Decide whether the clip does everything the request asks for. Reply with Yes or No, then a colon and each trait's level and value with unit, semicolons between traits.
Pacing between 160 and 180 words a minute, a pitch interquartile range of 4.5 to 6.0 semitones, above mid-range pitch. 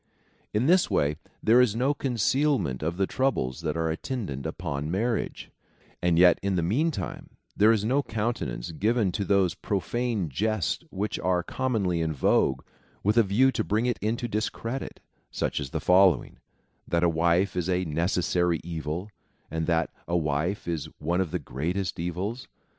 No: average, 165 wpm; average, 5.3 semitones; very low, 95 Hz